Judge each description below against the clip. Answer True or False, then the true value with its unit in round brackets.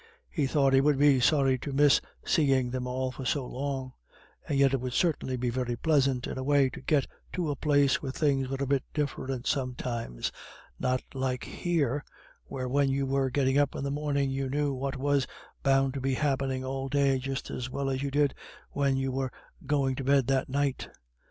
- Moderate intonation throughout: False (1.5 semitones)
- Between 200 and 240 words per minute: True (205 wpm)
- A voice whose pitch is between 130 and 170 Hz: True (135 Hz)